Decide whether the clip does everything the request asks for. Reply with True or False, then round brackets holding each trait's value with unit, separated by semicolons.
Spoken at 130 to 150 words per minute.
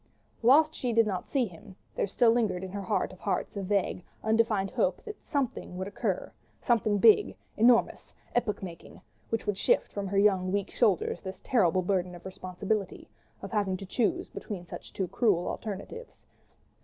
False (175 wpm)